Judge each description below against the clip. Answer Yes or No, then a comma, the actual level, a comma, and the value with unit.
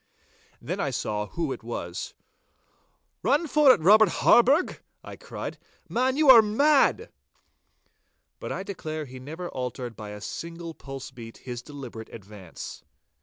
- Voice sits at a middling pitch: Yes, medium, 155 Hz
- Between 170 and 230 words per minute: No, average, 140 wpm